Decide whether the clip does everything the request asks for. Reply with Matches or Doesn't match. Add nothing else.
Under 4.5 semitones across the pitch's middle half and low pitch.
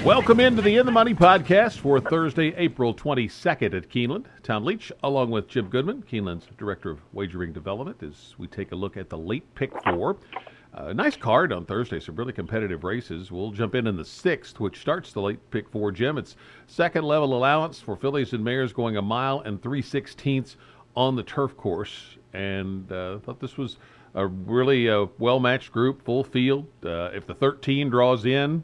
Doesn't match